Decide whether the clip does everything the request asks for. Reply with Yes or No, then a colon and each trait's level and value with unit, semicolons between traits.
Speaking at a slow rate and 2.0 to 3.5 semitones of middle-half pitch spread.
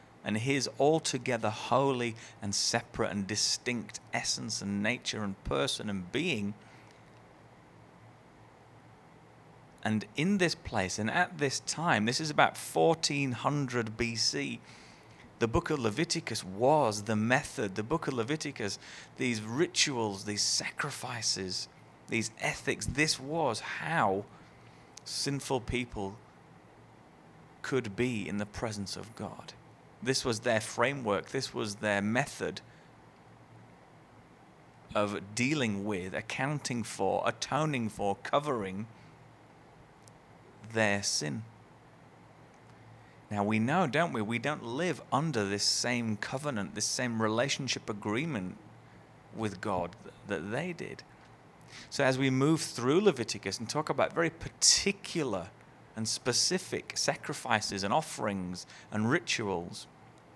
No: slow, 115 wpm; average, 4.5 semitones